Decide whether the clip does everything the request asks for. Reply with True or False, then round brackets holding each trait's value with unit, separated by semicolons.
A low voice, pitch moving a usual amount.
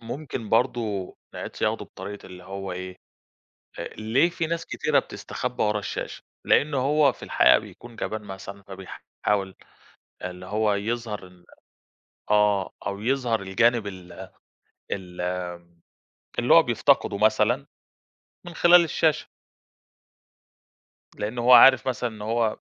True (105 Hz; 4.0 semitones)